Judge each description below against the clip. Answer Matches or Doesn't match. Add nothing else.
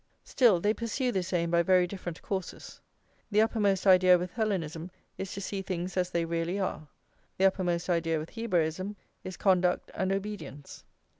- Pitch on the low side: Doesn't match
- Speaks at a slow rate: Doesn't match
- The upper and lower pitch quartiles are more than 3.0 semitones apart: Doesn't match